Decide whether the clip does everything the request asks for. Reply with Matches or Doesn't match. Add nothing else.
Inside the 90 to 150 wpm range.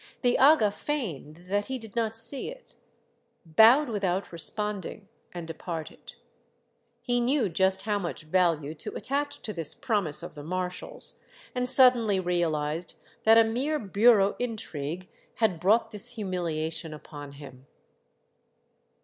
Matches